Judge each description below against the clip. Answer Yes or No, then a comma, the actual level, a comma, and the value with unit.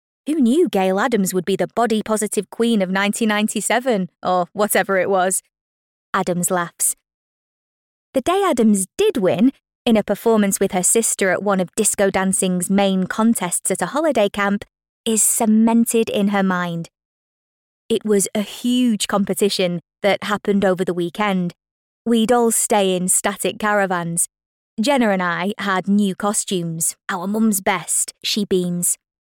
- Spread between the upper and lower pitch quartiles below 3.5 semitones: Yes, average, 3.1 semitones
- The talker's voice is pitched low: No, high, 200 Hz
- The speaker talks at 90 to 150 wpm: Yes, average, 145 wpm